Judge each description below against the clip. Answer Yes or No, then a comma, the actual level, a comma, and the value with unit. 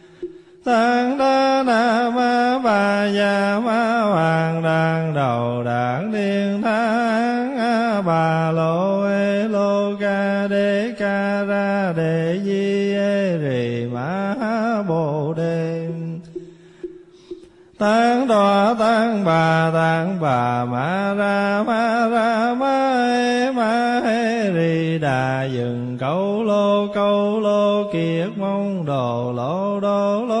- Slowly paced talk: Yes, slow, 115 wpm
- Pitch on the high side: Yes, high, 200 Hz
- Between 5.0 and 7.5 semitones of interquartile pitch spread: Yes, wide, 5.6 semitones